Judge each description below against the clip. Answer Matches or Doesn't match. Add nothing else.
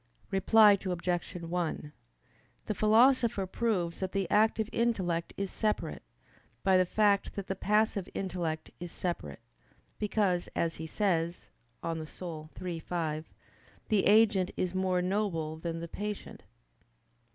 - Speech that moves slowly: Matches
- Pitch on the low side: Doesn't match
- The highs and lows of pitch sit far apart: Doesn't match